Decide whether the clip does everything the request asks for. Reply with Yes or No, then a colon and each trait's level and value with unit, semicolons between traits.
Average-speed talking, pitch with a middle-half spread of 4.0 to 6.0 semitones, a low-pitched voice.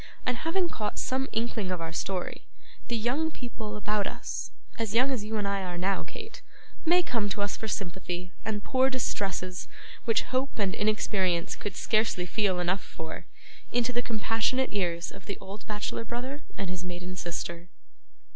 No: average, 175 wpm; average, 4.6 semitones; high, 210 Hz